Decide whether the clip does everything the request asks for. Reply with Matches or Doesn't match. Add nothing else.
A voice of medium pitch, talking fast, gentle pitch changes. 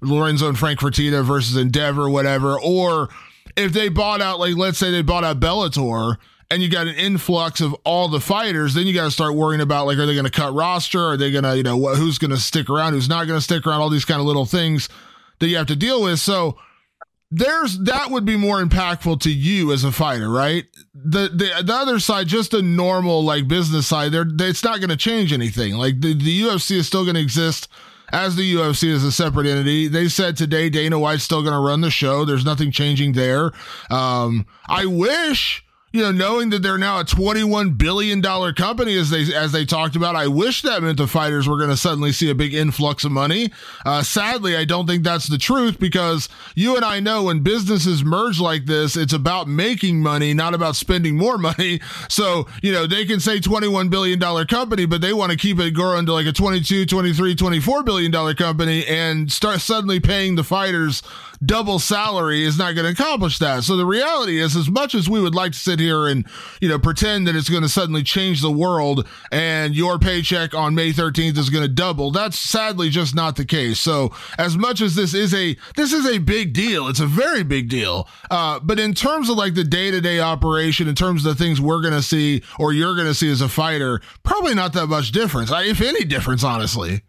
Doesn't match